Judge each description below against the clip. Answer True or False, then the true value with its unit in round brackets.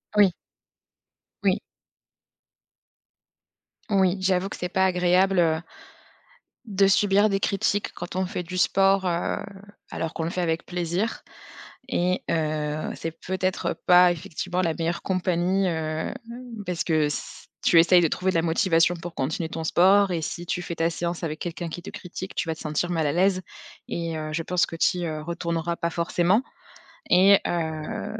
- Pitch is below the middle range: False (175 Hz)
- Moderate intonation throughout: False (2.2 semitones)